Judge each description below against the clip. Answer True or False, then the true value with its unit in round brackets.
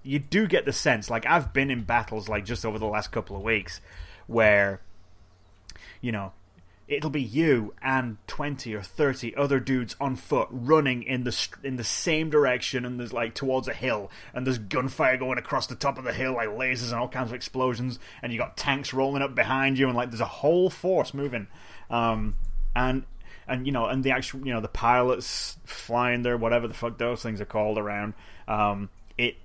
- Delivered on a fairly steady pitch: False (3.8 semitones)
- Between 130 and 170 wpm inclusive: False (205 wpm)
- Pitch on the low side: True (120 Hz)